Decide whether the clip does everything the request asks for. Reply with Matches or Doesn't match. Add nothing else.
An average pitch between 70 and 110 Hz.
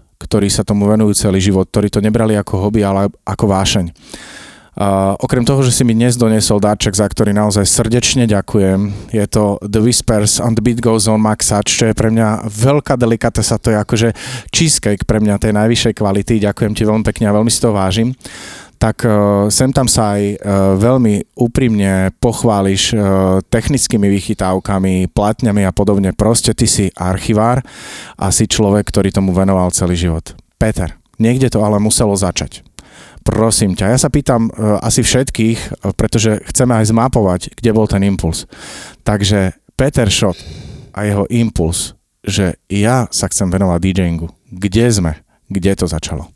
Matches